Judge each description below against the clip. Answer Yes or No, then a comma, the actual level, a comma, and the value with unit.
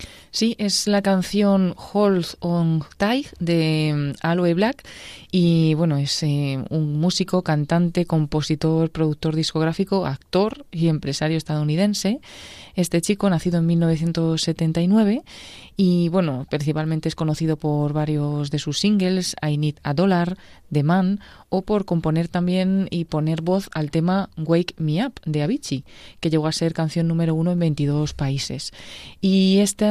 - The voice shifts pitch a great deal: No, average, 3.3 semitones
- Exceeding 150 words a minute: No, average, 140 wpm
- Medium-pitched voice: Yes, medium, 165 Hz